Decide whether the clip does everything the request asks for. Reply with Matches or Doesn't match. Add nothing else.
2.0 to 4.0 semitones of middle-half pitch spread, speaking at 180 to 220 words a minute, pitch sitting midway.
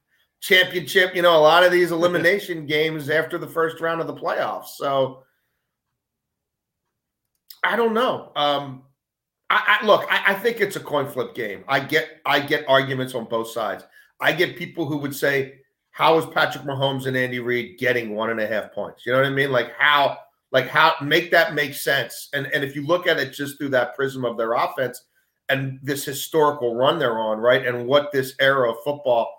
Matches